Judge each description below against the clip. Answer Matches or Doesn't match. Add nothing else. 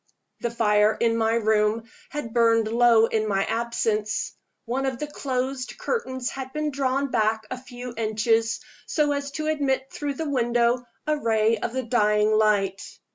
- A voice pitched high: Matches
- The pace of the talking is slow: Doesn't match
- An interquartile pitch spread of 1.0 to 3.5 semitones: Matches